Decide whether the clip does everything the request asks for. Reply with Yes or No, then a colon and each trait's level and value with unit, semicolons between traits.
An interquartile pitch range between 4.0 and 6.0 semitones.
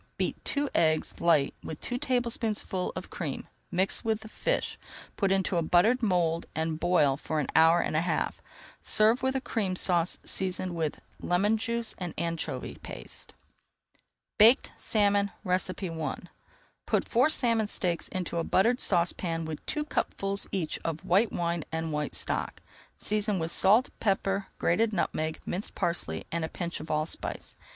Yes: average, 4.5 semitones